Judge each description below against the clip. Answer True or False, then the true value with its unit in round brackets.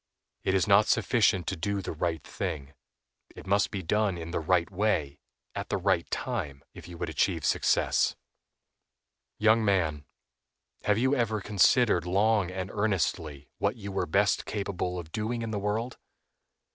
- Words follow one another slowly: False (160 wpm)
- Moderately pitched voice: False (95 Hz)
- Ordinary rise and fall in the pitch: True (4.1 semitones)